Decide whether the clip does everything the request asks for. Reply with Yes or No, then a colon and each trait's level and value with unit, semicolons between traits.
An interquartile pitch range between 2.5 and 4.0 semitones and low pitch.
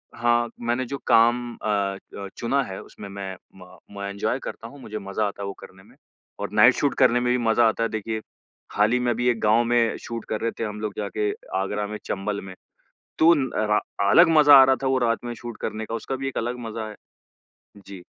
Yes: average, 2.8 semitones; low, 110 Hz